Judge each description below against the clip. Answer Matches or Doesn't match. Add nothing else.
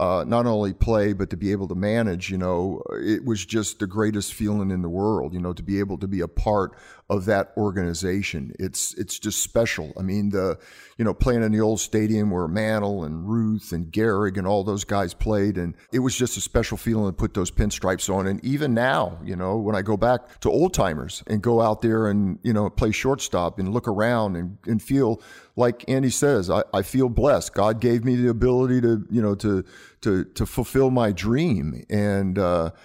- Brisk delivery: Matches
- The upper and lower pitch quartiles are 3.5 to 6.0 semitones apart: Doesn't match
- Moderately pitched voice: Doesn't match